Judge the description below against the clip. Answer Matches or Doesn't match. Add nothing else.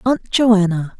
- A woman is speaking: Matches